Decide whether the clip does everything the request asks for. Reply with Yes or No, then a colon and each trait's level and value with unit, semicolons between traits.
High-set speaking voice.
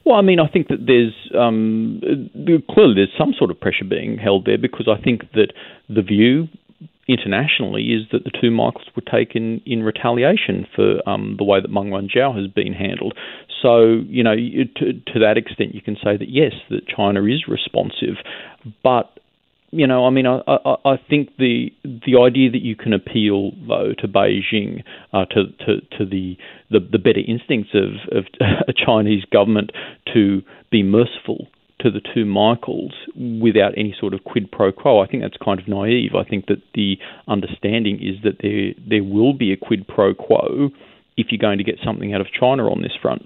No: low, 115 Hz